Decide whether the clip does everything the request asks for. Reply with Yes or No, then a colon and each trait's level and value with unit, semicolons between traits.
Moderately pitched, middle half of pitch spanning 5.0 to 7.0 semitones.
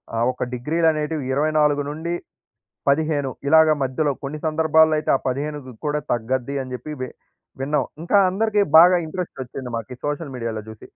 No: medium, 150 Hz; average, 3.3 semitones